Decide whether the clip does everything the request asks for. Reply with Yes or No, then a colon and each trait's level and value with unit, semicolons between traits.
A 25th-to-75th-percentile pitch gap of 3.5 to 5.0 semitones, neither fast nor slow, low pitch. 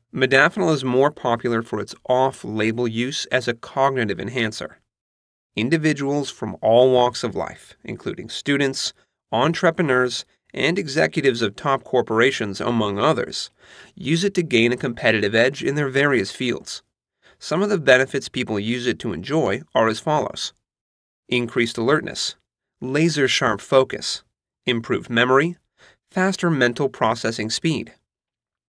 No: average, 3.8 semitones; slow, 125 wpm; low, 125 Hz